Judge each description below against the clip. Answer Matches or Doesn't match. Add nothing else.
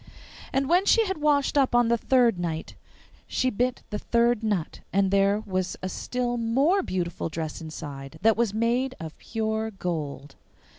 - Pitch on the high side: Matches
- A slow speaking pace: Doesn't match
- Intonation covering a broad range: Matches